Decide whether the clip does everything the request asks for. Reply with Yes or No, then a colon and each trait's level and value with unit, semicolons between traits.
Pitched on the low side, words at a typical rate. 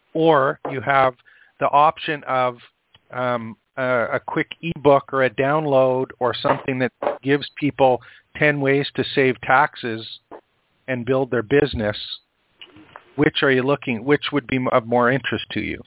Yes: low, 130 Hz; average, 150 wpm